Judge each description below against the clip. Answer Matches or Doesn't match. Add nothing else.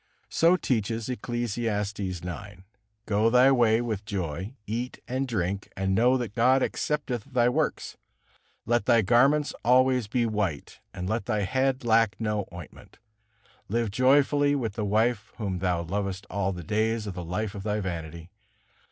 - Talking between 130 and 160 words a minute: Matches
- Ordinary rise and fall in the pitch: Matches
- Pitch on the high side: Doesn't match